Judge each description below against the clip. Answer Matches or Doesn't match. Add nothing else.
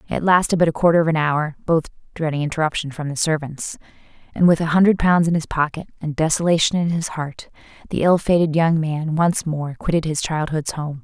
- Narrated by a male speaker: Doesn't match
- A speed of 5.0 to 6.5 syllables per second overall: Matches